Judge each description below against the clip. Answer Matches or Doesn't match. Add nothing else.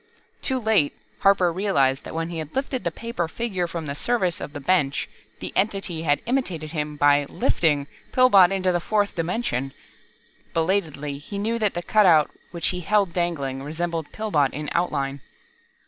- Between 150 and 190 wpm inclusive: Matches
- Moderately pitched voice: Matches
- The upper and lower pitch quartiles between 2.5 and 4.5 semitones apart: Doesn't match